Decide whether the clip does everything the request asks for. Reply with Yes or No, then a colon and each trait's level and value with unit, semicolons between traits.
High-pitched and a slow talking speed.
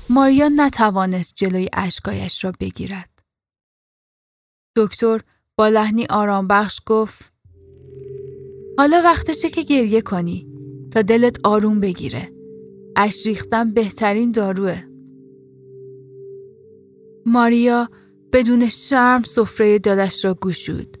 Yes: high, 210 Hz; slow, 90 wpm